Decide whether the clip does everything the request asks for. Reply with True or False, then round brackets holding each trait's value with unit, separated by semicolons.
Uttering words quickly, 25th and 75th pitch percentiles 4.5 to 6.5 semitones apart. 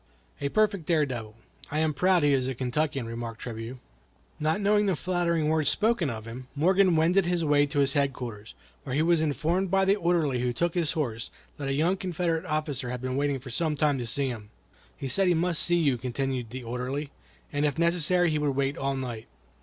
True (215 wpm; 4.9 semitones)